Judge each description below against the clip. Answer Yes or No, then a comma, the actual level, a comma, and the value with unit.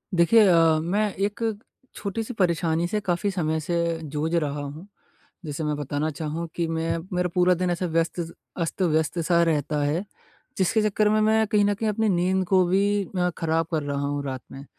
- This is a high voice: No, medium, 170 Hz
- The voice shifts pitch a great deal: No, average, 3.5 semitones